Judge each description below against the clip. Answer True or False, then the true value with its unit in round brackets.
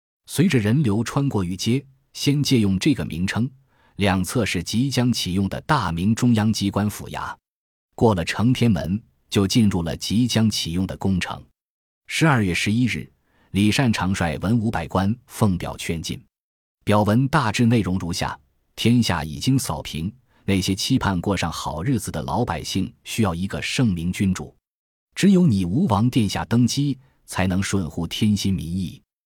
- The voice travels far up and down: False (4.8 semitones)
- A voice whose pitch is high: False (100 Hz)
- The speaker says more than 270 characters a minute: False (240 characters per minute)